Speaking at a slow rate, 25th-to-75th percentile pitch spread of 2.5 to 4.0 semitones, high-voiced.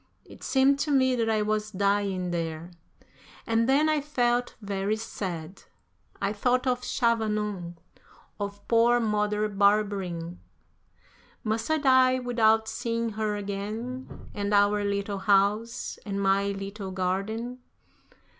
Yes: slow, 125 wpm; average, 3.0 semitones; high, 210 Hz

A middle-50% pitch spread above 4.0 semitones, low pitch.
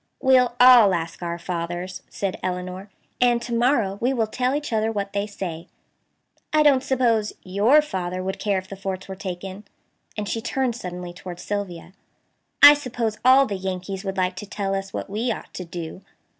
No: average, 4.6 semitones; high, 200 Hz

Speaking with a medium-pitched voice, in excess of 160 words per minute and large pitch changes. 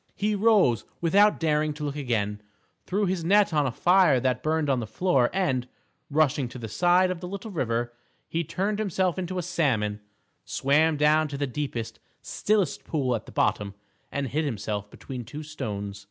Yes: medium, 150 Hz; average, 185 wpm; wide, 6.5 semitones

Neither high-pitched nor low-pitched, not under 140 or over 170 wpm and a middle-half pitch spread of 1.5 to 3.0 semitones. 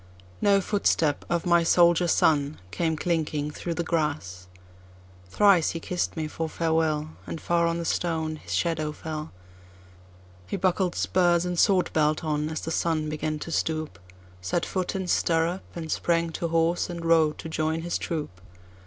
Yes: medium, 160 Hz; average, 155 wpm; average, 2.7 semitones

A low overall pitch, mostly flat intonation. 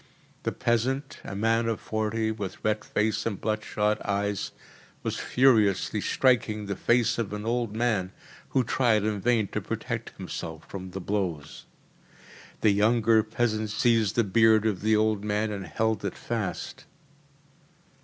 Yes: low, 110 Hz; narrow, 1.9 semitones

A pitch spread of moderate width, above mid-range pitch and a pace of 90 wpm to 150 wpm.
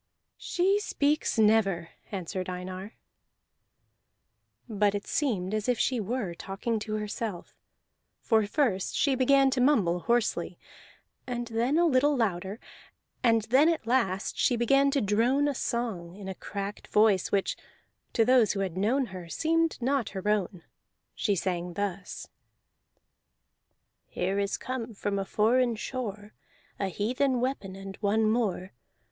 Yes: average, 4.6 semitones; high, 220 Hz; average, 140 wpm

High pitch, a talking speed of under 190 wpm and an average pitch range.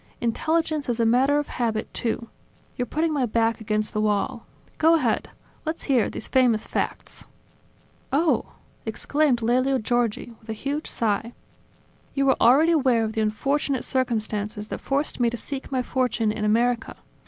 Yes: high, 240 Hz; average, 165 wpm; average, 3.8 semitones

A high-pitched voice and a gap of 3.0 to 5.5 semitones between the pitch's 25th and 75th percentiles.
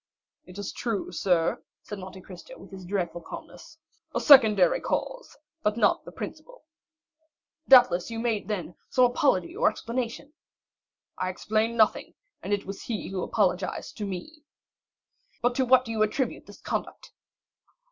Yes: high, 210 Hz; average, 4.7 semitones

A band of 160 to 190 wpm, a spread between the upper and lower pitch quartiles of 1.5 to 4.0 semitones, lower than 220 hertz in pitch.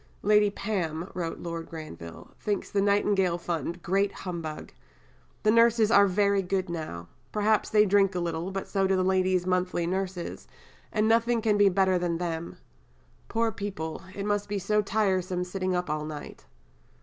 Yes: average, 170 wpm; average, 2.9 semitones; high, 190 Hz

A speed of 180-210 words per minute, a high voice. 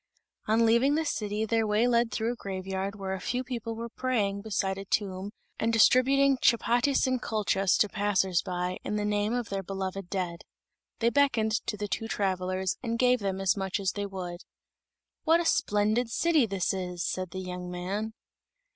Yes: average, 185 wpm; high, 205 Hz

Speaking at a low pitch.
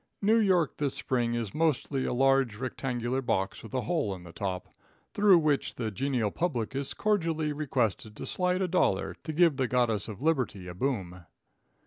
Yes: low, 130 Hz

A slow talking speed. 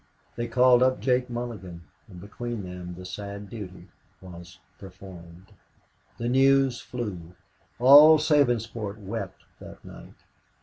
Yes: slow, 120 wpm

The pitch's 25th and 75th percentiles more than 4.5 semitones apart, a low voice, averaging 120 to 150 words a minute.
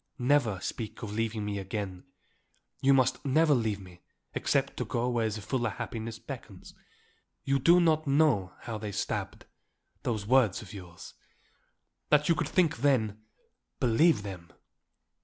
Yes: average, 5.1 semitones; low, 115 Hz; average, 145 wpm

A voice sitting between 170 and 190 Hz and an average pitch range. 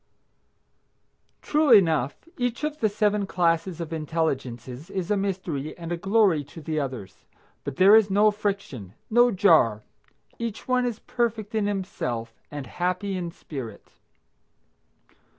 No: medium, 185 Hz; wide, 6.1 semitones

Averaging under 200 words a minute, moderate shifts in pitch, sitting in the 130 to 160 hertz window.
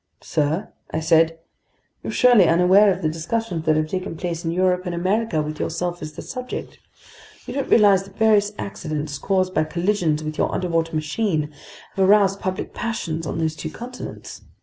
No: average, 175 wpm; average, 4.0 semitones; medium, 175 Hz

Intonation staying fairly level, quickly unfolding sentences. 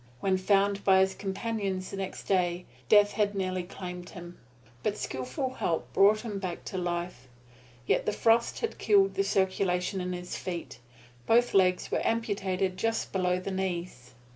No: narrow, 2.0 semitones; average, 165 wpm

